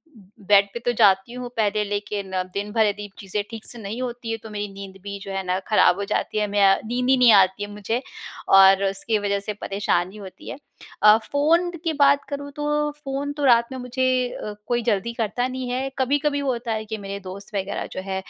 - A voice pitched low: No, high, 215 Hz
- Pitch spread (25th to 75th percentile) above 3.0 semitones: Yes, average, 3.9 semitones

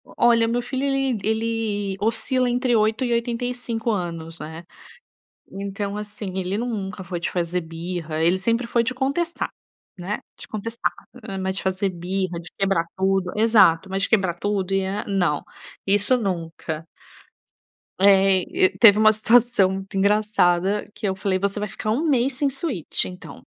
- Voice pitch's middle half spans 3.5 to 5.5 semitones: Yes, average, 3.8 semitones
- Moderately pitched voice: No, high, 200 Hz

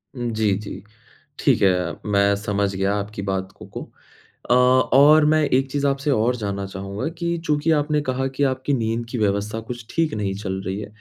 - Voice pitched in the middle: No, low, 110 Hz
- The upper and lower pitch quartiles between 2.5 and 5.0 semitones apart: No, wide, 5.5 semitones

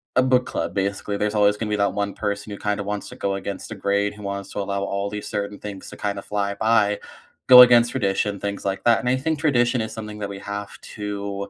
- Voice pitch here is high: No, low, 105 Hz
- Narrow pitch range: Yes, narrow, 1.3 semitones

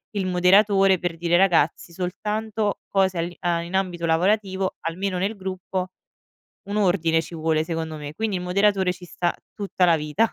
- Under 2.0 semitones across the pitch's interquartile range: No, narrow, 2.5 semitones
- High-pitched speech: No, medium, 180 Hz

